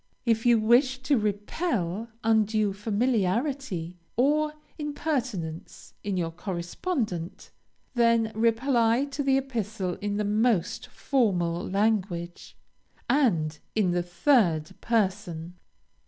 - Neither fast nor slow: No, slow, 100 wpm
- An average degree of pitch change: No, wide, 5.7 semitones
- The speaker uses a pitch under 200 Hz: No, high, 215 Hz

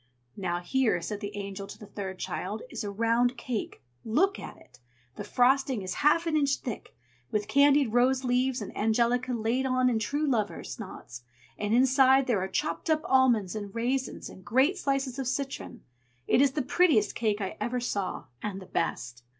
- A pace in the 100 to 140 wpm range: No, average, 185 wpm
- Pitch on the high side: Yes, high, 240 Hz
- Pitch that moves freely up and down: No, average, 4.4 semitones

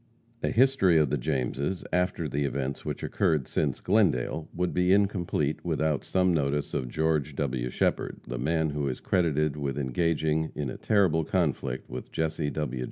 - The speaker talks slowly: No, average, 165 wpm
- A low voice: Yes, very low, 75 Hz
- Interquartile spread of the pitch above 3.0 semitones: Yes, average, 3.8 semitones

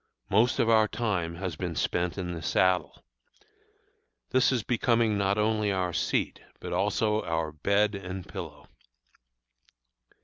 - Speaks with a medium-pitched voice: No, low, 100 Hz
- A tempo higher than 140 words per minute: No, slow, 135 wpm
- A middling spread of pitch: Yes, average, 3.5 semitones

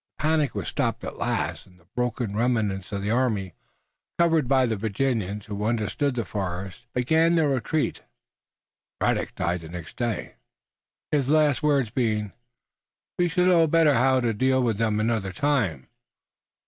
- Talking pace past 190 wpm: No, average, 160 wpm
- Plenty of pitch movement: Yes, wide, 5.7 semitones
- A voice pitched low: Yes, low, 120 Hz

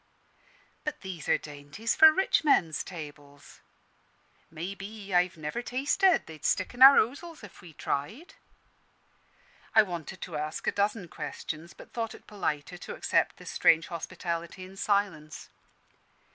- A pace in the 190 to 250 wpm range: No, average, 145 wpm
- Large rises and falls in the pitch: Yes, wide, 5.9 semitones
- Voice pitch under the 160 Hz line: No, medium, 185 Hz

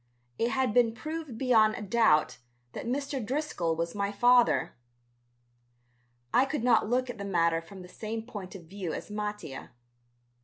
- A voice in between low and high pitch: No, high, 215 Hz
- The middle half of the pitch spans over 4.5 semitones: Yes, average, 5.0 semitones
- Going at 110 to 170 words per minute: Yes, average, 160 wpm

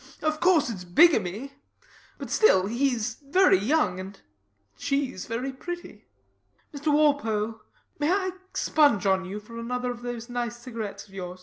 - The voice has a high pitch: Yes, high, 240 Hz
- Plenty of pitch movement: Yes, wide, 5.8 semitones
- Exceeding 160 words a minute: No, average, 145 wpm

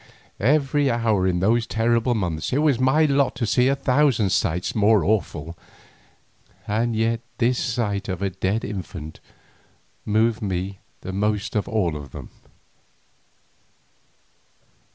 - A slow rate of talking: Yes, slow, 130 wpm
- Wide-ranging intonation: No, average, 4.2 semitones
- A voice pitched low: Yes, low, 110 Hz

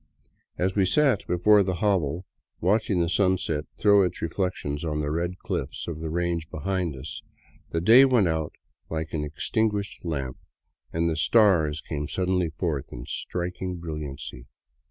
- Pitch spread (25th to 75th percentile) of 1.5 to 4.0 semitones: Yes, average, 3.6 semitones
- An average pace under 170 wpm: Yes, average, 155 wpm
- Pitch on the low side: Yes, very low, 85 Hz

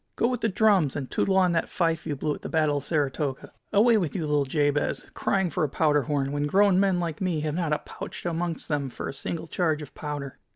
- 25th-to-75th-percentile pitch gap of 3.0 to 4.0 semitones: Yes, average, 3.7 semitones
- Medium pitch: Yes, medium, 155 Hz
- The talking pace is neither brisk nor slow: No, fast, 245 wpm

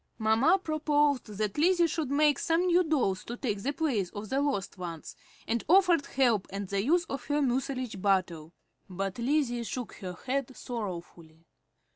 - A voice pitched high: Yes, high, 245 Hz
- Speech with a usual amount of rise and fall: No, wide, 6.9 semitones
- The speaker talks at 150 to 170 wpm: Yes, average, 165 wpm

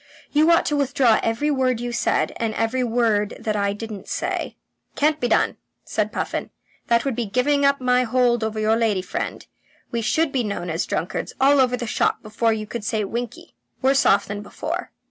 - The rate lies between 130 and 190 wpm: No, fast, 205 wpm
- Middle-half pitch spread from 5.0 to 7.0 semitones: No, average, 3.3 semitones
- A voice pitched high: Yes, high, 235 Hz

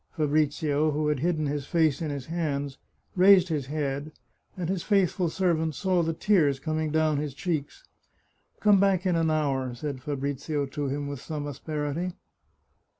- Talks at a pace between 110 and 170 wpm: Yes, average, 165 wpm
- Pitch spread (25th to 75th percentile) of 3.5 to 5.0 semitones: No, average, 3.0 semitones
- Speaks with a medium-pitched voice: Yes, medium, 155 Hz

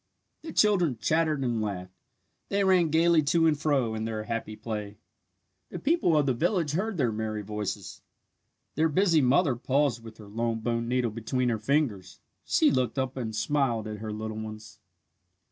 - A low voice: Yes, low, 125 Hz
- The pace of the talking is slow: No, average, 175 wpm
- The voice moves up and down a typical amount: No, wide, 6.0 semitones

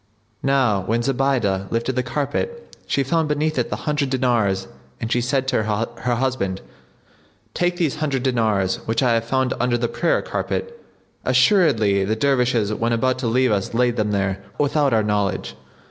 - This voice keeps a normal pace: Yes, average, 170 wpm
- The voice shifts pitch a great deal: No, average, 4.1 semitones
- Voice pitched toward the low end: Yes, low, 125 Hz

